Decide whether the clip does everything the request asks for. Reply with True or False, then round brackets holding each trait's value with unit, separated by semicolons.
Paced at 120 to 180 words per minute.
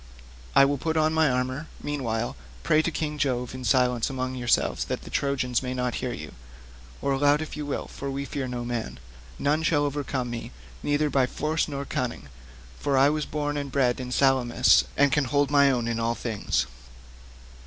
False (190 wpm)